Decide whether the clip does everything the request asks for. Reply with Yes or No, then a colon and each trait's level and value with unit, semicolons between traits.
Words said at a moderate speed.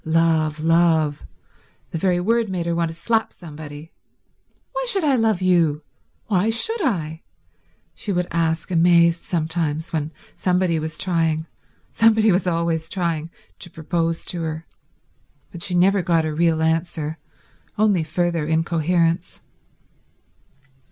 No: slow, 125 wpm